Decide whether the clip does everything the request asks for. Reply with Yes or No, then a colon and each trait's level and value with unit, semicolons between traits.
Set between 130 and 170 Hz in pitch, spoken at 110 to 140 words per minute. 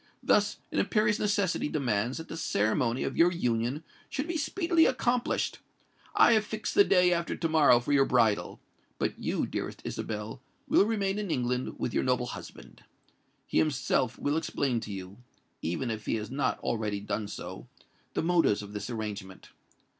No: low, 135 Hz; average, 160 wpm